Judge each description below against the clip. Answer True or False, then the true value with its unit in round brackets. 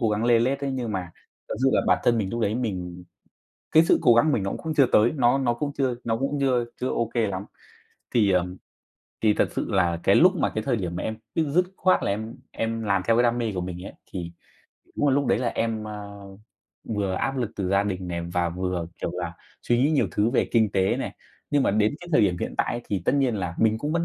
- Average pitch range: True (5.0 semitones)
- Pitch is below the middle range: True (110 Hz)